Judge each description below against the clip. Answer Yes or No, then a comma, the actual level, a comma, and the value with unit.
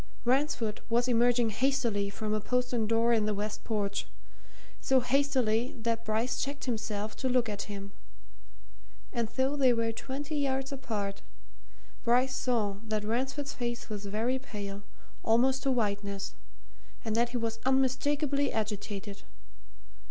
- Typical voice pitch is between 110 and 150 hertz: No, high, 235 Hz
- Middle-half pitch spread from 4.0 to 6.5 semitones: No, average, 3.6 semitones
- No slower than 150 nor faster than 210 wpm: No, slow, 135 wpm